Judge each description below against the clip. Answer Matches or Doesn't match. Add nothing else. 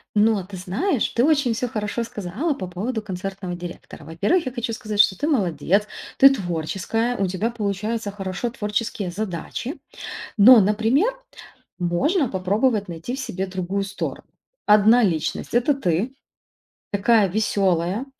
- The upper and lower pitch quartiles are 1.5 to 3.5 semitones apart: Doesn't match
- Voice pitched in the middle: Doesn't match